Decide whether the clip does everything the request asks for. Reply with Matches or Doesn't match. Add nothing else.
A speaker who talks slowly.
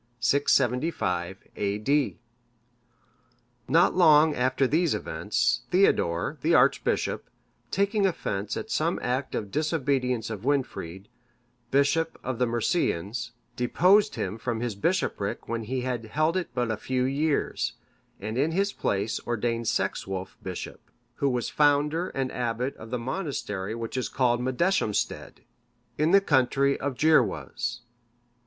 Matches